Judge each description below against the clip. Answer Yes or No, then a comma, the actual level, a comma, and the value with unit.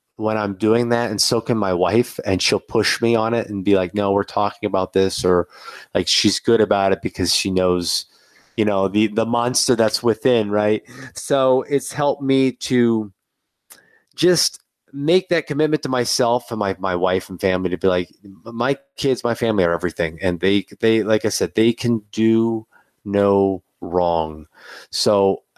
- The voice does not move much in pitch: No, average, 3.8 semitones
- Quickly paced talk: No, average, 185 wpm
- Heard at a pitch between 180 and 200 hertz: No, low, 110 Hz